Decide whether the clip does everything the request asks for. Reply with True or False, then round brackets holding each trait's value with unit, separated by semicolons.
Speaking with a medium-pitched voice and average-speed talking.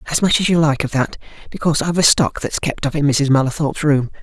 False (150 Hz; 255 wpm)